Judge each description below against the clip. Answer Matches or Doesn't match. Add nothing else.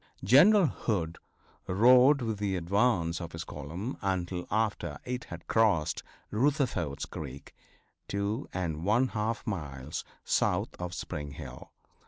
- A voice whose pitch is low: Matches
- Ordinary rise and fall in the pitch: Doesn't match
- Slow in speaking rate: Matches